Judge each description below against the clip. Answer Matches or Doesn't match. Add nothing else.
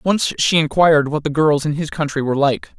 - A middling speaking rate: Doesn't match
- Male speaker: Matches